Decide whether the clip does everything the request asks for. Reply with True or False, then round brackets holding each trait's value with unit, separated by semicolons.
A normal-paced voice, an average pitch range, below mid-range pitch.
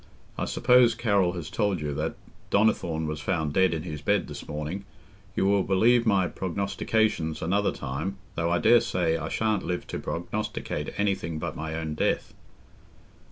True (160 wpm; 4.3 semitones; 90 Hz)